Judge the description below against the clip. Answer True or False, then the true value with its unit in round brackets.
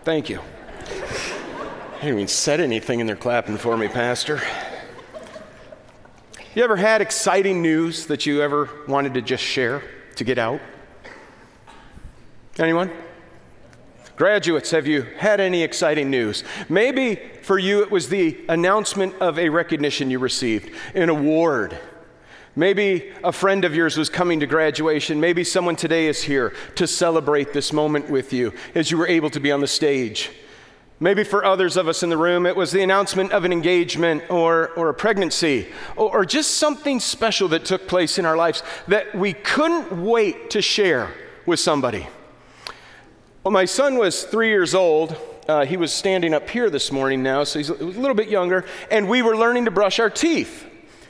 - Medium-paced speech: True (175 wpm)